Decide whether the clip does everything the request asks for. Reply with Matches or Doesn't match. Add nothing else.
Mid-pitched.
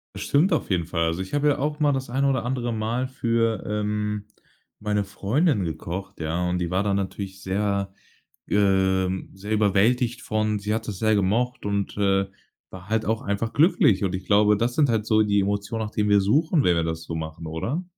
Doesn't match